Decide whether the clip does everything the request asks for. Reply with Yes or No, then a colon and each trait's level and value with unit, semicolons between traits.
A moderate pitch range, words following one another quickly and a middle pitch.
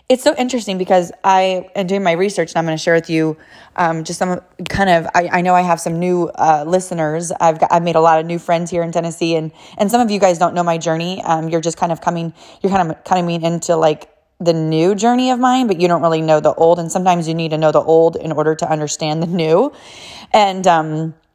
No: narrow, 2.2 semitones; fast, 260 wpm; medium, 170 Hz